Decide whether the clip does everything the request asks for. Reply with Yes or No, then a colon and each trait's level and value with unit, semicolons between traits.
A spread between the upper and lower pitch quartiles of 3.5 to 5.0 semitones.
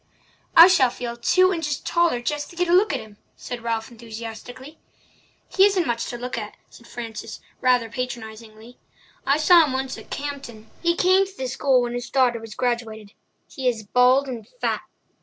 Yes: average, 4.2 semitones